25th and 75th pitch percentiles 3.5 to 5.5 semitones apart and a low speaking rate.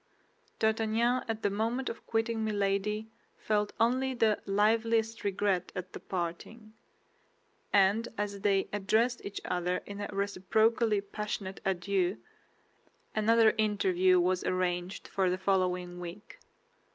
No: average, 2.9 semitones; slow, 120 wpm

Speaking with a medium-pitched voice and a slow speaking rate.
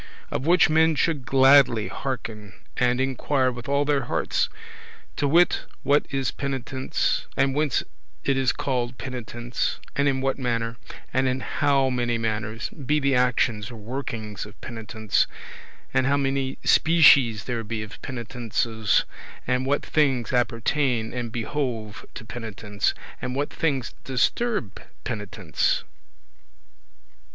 No: low, 125 Hz; slow, 130 wpm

